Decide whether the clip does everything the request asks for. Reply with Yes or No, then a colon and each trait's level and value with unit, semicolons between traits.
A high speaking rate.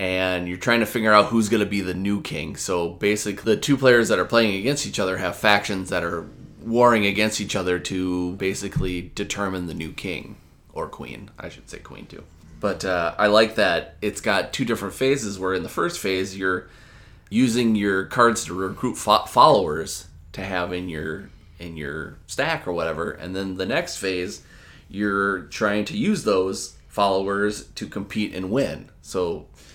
No: average, 190 wpm